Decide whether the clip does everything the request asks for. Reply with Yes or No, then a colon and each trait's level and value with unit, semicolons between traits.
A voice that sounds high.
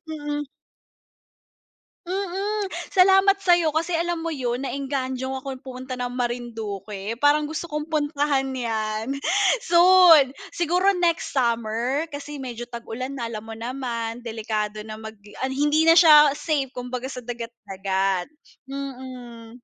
Yes: very high, 260 Hz